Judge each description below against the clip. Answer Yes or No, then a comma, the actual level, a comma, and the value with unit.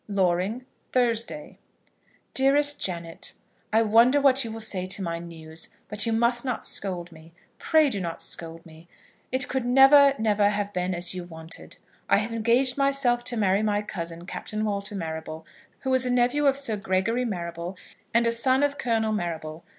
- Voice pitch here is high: Yes, high, 215 Hz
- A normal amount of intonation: No, wide, 6.2 semitones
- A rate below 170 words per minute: No, average, 175 wpm